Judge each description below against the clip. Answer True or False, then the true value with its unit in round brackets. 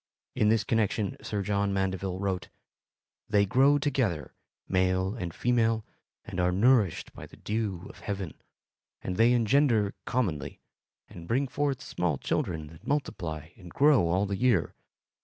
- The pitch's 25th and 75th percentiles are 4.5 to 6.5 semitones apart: True (4.9 semitones)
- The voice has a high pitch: False (100 Hz)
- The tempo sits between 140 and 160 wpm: True (145 wpm)